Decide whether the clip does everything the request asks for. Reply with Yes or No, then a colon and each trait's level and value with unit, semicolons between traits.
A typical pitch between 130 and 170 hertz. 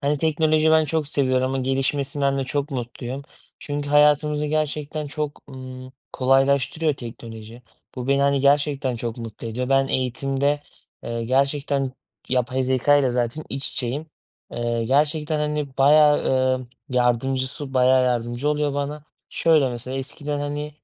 Yes: low, 135 Hz